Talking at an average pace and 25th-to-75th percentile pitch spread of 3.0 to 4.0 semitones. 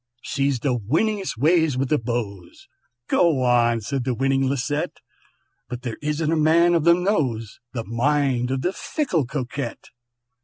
No: average, 155 wpm; average, 4.6 semitones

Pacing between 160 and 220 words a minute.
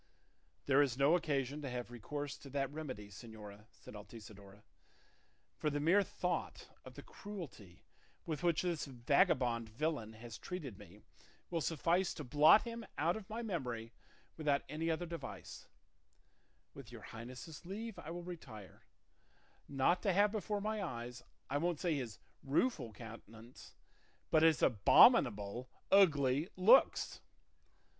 No: average, 140 wpm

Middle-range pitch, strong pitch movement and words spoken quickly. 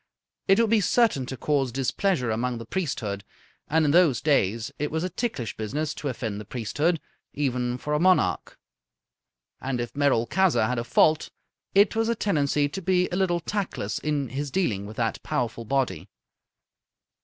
No: medium, 145 Hz; wide, 6.7 semitones; average, 170 wpm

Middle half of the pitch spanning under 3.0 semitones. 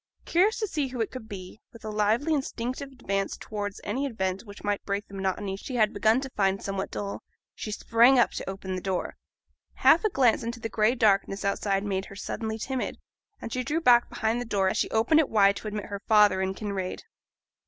No: average, 3.7 semitones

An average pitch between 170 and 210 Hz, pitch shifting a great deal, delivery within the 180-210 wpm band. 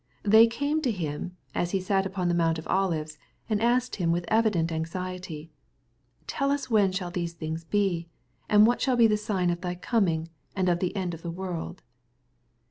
No: medium, 185 Hz; average, 4.0 semitones; average, 200 wpm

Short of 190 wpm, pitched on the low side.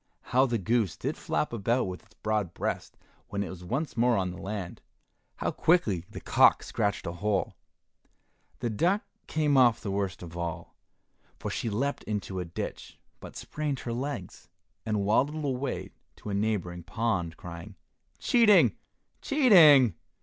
Yes: average, 155 wpm; low, 110 Hz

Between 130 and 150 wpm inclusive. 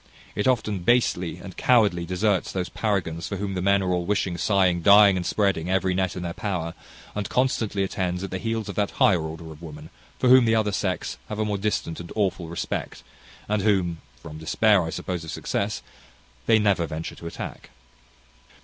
No: average, 195 wpm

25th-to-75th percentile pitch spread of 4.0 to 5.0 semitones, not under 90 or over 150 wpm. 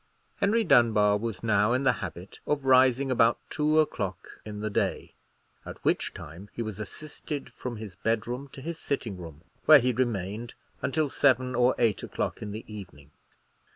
No: average, 4.4 semitones; average, 170 wpm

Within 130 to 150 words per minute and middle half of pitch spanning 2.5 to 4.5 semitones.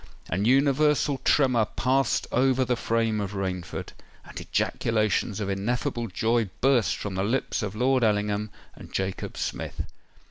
Yes: average, 140 wpm; average, 4.0 semitones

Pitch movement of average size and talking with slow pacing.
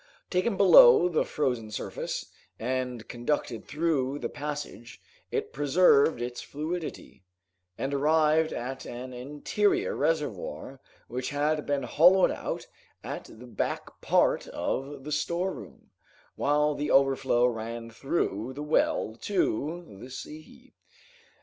Yes: average, 4.4 semitones; slow, 120 wpm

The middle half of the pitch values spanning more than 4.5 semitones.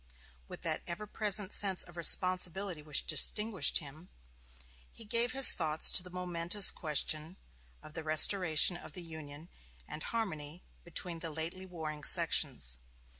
No: average, 3.5 semitones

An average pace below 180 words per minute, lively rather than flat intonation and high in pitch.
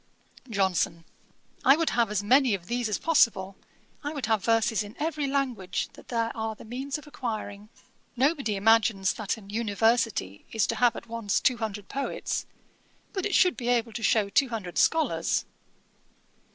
No: average, 170 wpm; average, 4.2 semitones; high, 225 Hz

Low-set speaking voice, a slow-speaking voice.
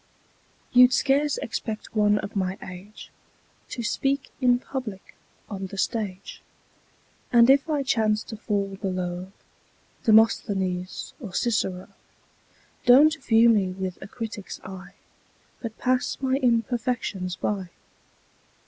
No: high, 215 Hz; slow, 115 wpm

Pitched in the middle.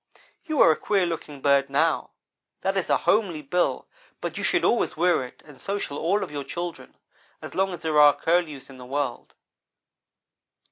Yes: medium, 160 Hz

